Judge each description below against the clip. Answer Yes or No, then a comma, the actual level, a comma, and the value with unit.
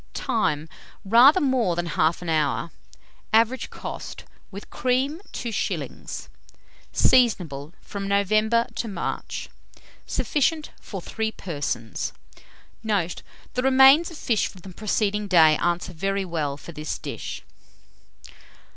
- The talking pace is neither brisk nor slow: No, slow, 110 wpm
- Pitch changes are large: Yes, wide, 5.9 semitones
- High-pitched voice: Yes, high, 200 Hz